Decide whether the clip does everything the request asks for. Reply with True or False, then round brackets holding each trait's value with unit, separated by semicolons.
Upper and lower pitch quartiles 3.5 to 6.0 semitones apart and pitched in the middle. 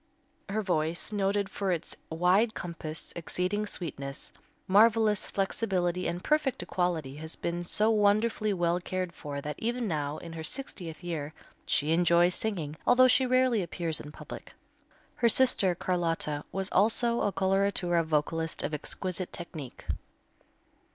True (4.2 semitones; 180 Hz)